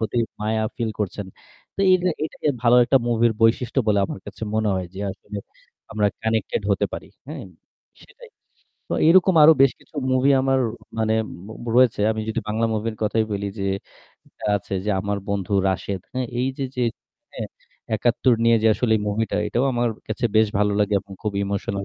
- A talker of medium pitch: No, low, 110 Hz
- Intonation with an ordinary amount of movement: Yes, average, 3.1 semitones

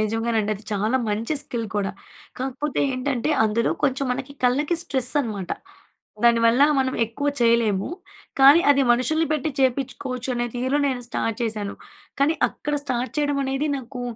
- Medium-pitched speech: No, very high, 250 Hz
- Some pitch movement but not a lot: Yes, average, 3.2 semitones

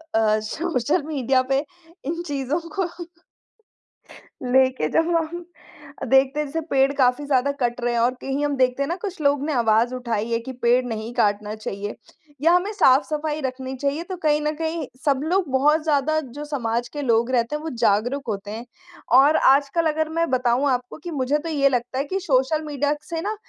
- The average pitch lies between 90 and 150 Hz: No, very high, 275 Hz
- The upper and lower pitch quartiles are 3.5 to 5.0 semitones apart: Yes, average, 3.8 semitones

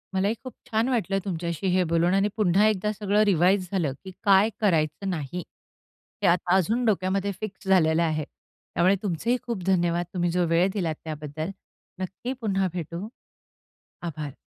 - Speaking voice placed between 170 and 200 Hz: Yes, medium, 185 Hz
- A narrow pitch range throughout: No, average, 3.1 semitones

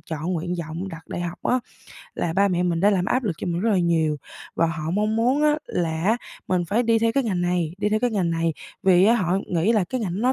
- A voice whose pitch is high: No, medium, 180 Hz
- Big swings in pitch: No, average, 4.5 semitones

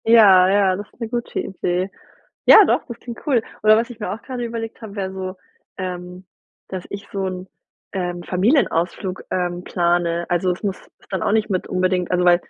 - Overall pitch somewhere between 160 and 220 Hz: Yes, high, 190 Hz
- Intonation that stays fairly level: No, average, 3.2 semitones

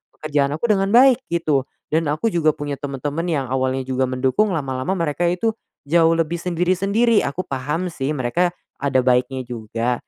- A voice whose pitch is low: No, medium, 150 Hz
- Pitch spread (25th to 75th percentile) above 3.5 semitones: Yes, average, 4.9 semitones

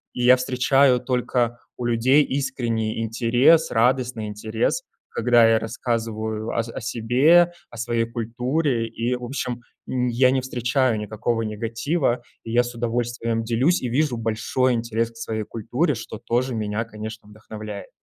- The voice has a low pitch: Yes, low, 120 Hz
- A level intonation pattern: Yes, narrow, 2.1 semitones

